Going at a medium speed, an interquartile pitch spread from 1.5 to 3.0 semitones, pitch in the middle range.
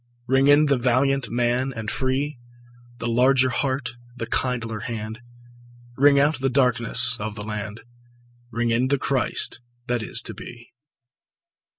No: average, 145 wpm; narrow, 2.6 semitones; low, 125 Hz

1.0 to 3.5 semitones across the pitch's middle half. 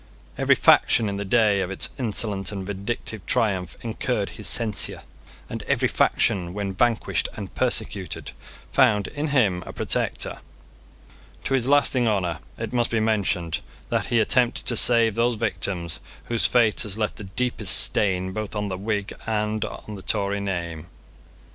Yes: average, 3.1 semitones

